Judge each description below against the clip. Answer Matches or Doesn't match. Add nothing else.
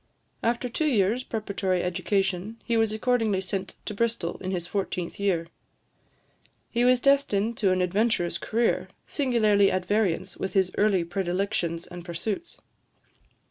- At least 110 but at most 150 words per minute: Matches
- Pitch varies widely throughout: Doesn't match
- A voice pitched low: Doesn't match